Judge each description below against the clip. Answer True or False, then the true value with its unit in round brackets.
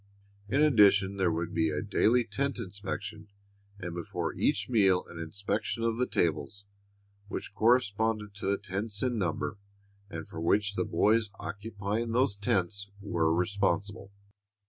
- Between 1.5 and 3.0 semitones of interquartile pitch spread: True (2.7 semitones)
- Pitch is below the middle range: True (100 Hz)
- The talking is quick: False (145 wpm)